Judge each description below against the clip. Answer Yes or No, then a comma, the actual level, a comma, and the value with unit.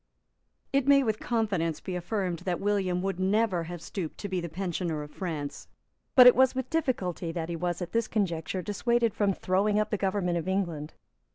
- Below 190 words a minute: No, average, 195 wpm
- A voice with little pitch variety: No, average, 3.7 semitones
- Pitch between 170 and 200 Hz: Yes, medium, 185 Hz